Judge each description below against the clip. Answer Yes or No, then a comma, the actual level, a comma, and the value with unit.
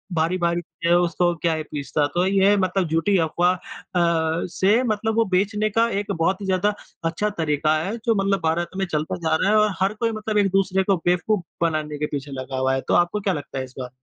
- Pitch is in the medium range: Yes, medium, 180 Hz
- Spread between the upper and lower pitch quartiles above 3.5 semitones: Yes, average, 3.9 semitones